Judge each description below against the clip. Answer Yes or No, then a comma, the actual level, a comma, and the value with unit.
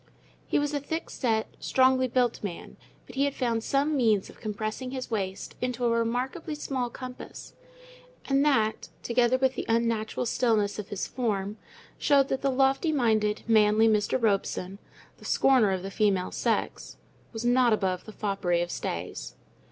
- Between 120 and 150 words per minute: No, average, 165 wpm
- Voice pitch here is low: No, high, 230 Hz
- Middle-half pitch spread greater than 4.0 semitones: No, average, 3.7 semitones